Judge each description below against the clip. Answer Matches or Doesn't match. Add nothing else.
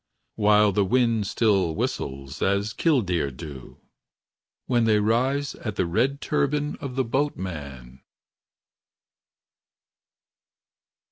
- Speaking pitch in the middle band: Doesn't match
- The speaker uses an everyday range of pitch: Doesn't match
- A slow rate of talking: Matches